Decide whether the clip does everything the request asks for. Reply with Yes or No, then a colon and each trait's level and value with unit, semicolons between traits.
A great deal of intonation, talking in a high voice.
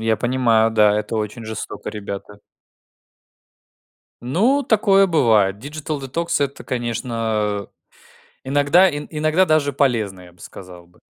No: wide, 6.2 semitones; low, 120 Hz